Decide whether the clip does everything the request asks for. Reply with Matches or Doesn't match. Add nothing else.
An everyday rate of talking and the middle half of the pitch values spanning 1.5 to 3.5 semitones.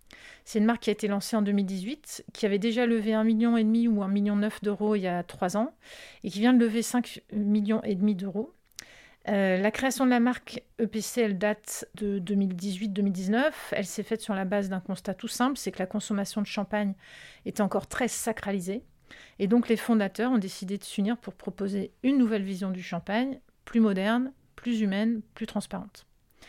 Matches